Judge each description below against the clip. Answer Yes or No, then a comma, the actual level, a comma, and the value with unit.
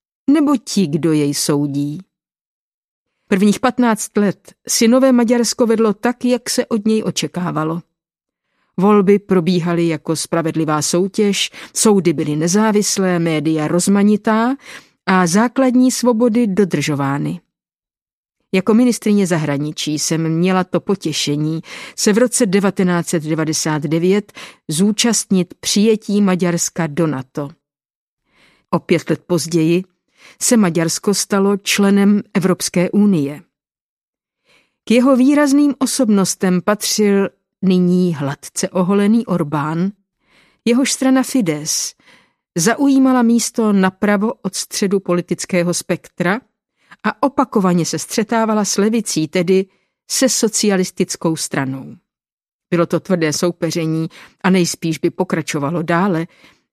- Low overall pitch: No, high, 190 Hz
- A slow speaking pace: Yes, slow, 100 wpm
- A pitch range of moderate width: Yes, average, 4.8 semitones